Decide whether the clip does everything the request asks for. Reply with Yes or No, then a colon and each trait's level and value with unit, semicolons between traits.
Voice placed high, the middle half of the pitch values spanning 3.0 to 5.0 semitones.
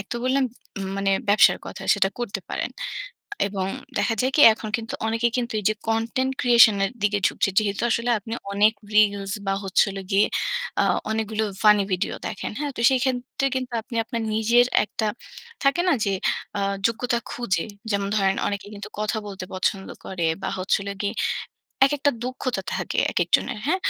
Yes: high, 220 Hz; average, 3.4 semitones